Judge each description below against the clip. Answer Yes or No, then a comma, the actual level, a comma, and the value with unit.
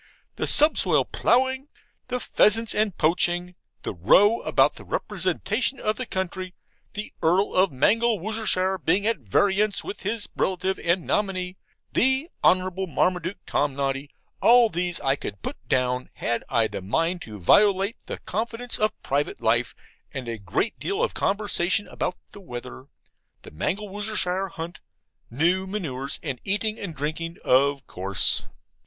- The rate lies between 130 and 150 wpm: Yes, average, 140 wpm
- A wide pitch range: Yes, wide, 6.8 semitones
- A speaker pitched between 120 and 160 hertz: No, medium, 185 Hz